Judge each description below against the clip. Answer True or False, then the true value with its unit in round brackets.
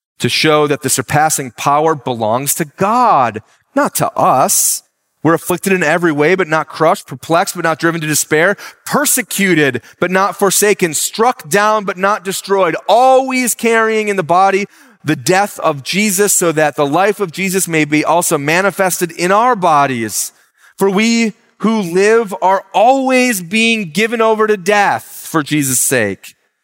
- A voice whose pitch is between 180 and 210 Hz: True (190 Hz)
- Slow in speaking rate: False (160 wpm)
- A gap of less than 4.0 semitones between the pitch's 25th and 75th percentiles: False (5.1 semitones)